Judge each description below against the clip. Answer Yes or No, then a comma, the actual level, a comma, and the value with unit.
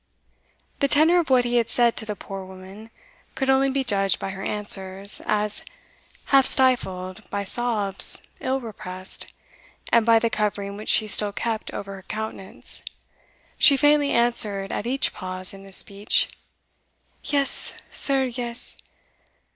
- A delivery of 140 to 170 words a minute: Yes, average, 145 wpm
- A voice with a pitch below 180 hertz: No, high, 215 Hz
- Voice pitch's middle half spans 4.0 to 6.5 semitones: Yes, average, 4.5 semitones